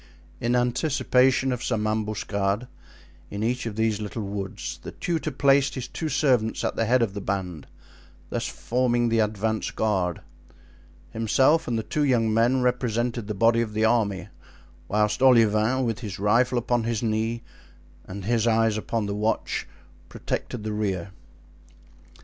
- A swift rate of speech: No, average, 155 wpm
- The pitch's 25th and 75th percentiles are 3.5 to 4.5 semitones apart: No, average, 2.7 semitones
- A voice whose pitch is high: No, low, 115 Hz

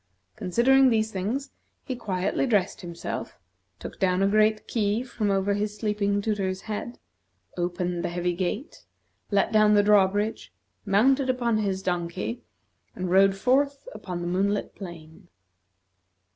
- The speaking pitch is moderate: No, high, 205 Hz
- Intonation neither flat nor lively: Yes, average, 3.1 semitones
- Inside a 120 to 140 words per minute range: Yes, slow, 135 wpm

